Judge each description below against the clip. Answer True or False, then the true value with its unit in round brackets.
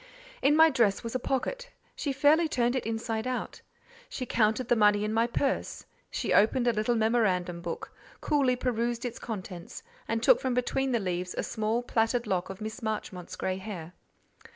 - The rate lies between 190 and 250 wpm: False (180 wpm)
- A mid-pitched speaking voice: False (230 Hz)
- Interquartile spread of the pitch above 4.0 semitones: False (3.3 semitones)